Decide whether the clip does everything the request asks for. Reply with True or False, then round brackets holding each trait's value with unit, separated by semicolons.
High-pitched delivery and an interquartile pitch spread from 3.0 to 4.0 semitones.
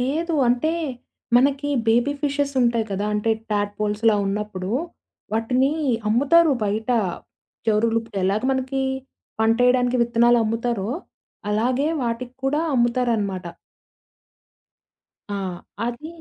True (240 Hz; 3.5 semitones)